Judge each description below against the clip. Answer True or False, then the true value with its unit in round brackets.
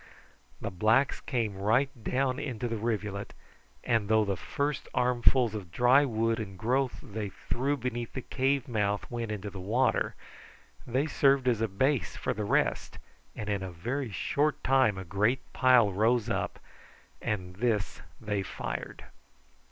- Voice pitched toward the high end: False (115 Hz)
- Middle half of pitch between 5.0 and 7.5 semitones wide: False (3.9 semitones)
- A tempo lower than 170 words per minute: True (155 wpm)